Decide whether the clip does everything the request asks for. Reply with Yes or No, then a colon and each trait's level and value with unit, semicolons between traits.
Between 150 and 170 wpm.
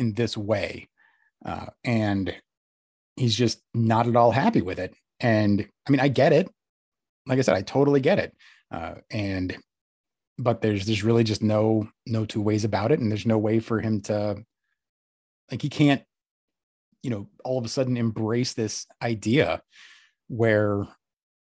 Yes: average, 165 wpm